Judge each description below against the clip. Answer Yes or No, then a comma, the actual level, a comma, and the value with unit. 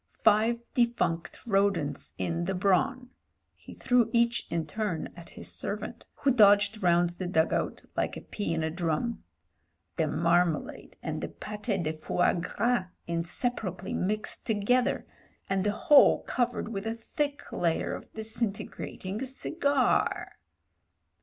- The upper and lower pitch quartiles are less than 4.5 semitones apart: No, wide, 5.5 semitones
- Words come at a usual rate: Yes, average, 145 wpm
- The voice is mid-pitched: No, high, 200 Hz